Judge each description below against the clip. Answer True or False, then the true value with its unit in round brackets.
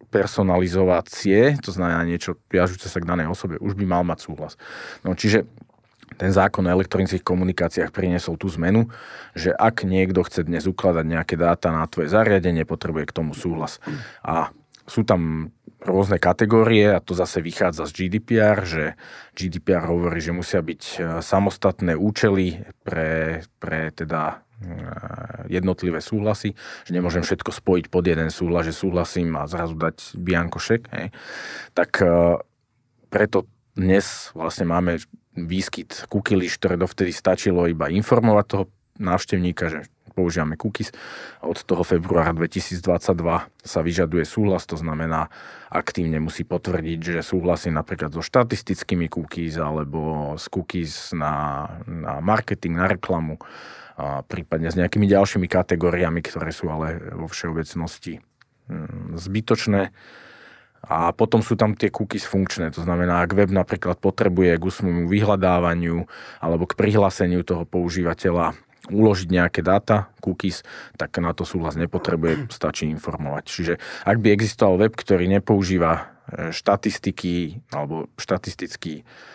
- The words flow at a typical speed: True (130 wpm)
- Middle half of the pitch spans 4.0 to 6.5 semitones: False (2.9 semitones)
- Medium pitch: False (90 Hz)